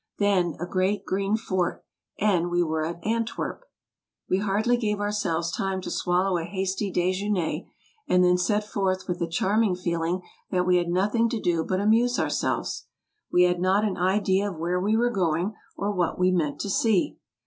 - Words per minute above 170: Yes, average, 180 wpm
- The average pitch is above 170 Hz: Yes, medium, 185 Hz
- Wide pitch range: No, average, 2.7 semitones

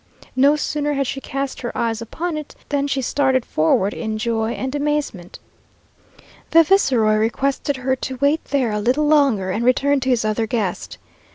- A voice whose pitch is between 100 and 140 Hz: No, very high, 260 Hz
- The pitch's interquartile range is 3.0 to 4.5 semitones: Yes, average, 4.2 semitones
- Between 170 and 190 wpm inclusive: Yes, average, 175 wpm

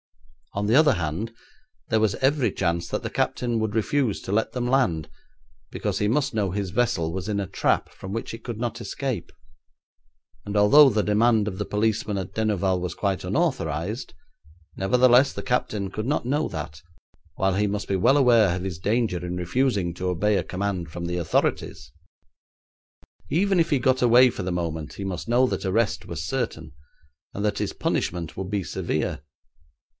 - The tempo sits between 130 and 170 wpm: No, average, 185 wpm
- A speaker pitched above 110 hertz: No, low, 105 Hz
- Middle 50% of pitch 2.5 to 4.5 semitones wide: No, average, 4.9 semitones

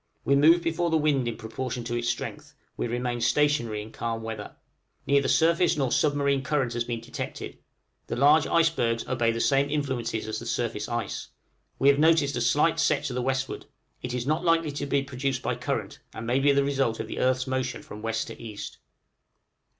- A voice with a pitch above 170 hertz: No, low, 130 Hz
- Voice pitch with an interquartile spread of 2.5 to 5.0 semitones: Yes, average, 3.5 semitones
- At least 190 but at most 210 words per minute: Yes, average, 200 wpm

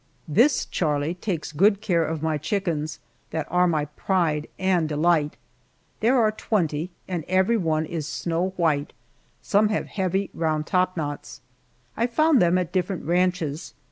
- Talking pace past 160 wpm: No, average, 145 wpm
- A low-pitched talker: No, medium, 175 Hz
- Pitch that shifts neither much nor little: Yes, average, 3.5 semitones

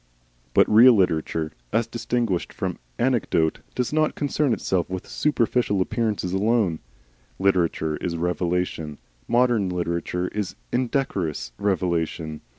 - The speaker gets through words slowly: Yes, slow, 110 wpm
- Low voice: Yes, very low, 95 Hz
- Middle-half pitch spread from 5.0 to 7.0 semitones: Yes, wide, 5.6 semitones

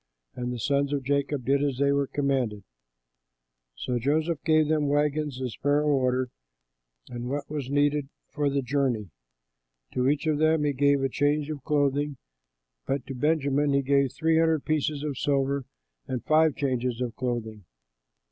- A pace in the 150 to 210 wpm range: Yes, average, 165 wpm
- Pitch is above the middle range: No, medium, 140 Hz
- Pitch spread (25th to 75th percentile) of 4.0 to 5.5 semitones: No, narrow, 2.4 semitones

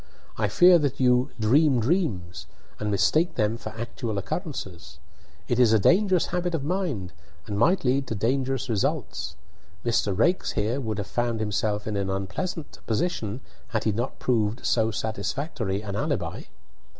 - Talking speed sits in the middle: Yes, average, 155 wpm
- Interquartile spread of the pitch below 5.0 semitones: No, average, 5.3 semitones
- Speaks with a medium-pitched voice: No, low, 115 Hz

